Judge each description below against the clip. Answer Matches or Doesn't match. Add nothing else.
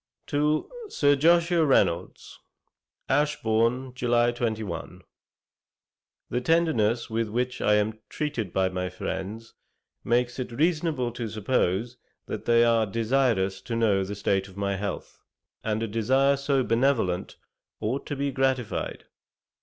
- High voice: Doesn't match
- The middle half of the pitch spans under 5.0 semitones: Matches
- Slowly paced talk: Matches